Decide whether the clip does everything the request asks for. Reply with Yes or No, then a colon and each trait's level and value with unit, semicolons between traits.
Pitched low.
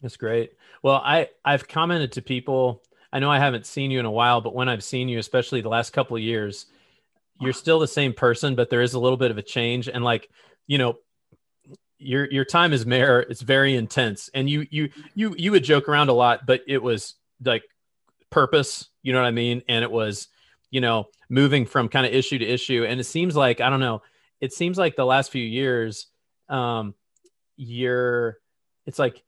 Yes: low, 130 Hz